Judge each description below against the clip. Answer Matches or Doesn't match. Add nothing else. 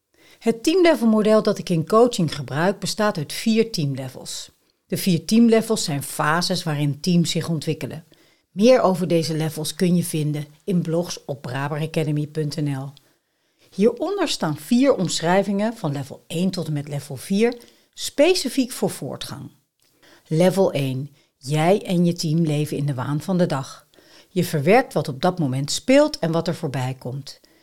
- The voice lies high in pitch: Doesn't match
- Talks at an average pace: Matches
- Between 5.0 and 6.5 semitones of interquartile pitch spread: Matches